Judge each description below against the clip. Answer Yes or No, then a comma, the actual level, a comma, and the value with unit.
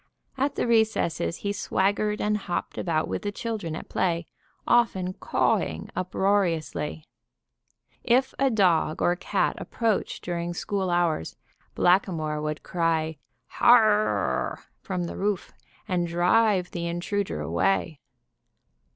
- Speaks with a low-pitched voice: No, medium, 185 Hz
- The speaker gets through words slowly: Yes, slow, 125 wpm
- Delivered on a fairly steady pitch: No, average, 3.7 semitones